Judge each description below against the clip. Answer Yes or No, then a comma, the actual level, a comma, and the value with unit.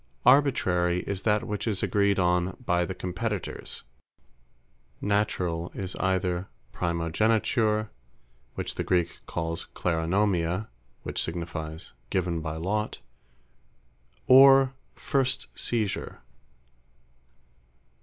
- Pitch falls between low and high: No, very low, 95 Hz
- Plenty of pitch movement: No, average, 3.6 semitones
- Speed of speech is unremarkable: No, slow, 90 wpm